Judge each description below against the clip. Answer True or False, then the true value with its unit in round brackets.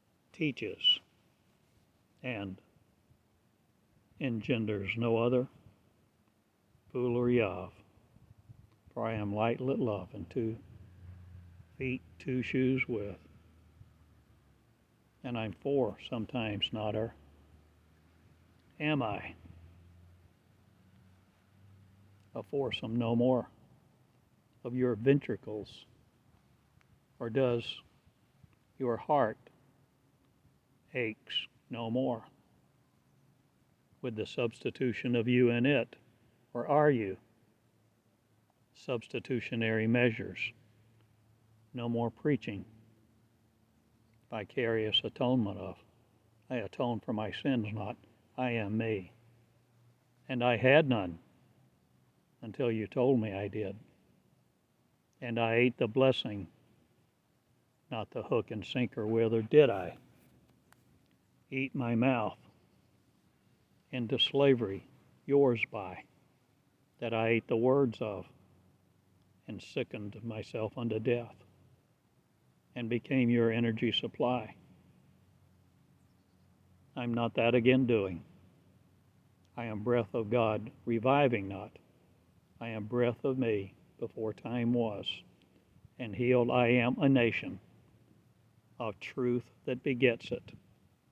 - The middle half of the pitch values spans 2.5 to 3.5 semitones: True (3.2 semitones)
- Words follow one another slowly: True (95 wpm)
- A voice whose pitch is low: True (115 Hz)